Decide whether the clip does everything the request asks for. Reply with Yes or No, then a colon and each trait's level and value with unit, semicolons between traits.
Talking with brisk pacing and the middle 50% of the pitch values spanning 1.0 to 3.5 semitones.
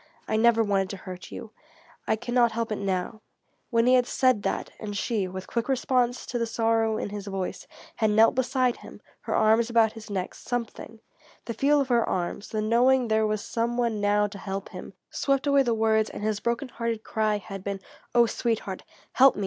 Yes: fast, 210 wpm; narrow, 2.5 semitones